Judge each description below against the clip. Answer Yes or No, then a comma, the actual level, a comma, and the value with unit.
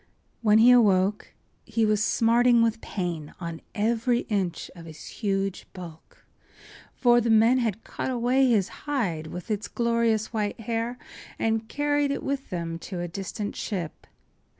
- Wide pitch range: No, average, 4.2 semitones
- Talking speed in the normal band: Yes, average, 150 wpm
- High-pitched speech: Yes, high, 220 Hz